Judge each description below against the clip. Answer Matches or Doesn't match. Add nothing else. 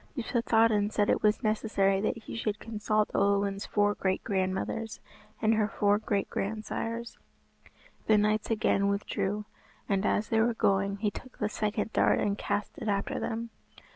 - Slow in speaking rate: Doesn't match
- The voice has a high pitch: Matches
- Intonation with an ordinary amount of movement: Doesn't match